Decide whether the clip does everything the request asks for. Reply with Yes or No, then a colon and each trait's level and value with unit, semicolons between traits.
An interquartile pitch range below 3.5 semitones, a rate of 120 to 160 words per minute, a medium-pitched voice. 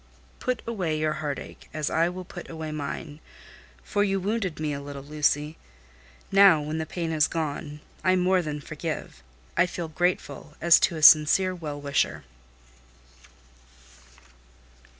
Yes: average, 3.1 semitones; average, 150 wpm; medium, 160 Hz